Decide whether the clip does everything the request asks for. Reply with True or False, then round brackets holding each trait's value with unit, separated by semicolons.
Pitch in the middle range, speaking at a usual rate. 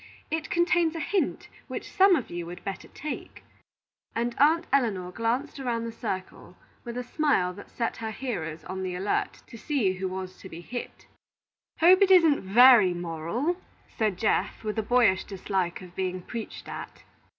False (225 Hz; 175 wpm)